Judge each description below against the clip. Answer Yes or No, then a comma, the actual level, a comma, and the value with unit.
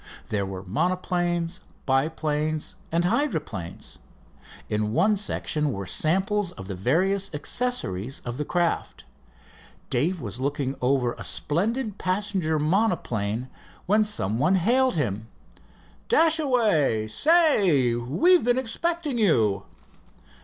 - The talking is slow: Yes, slow, 110 wpm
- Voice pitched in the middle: Yes, medium, 160 Hz